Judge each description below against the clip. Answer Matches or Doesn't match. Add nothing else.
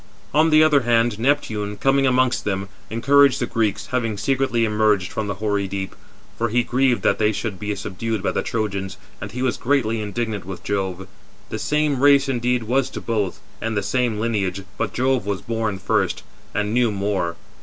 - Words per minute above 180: Matches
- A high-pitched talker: Doesn't match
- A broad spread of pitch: Doesn't match